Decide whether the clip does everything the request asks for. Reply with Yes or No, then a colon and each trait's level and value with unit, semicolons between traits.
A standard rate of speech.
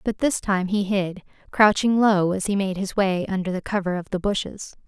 No: fast, 220 wpm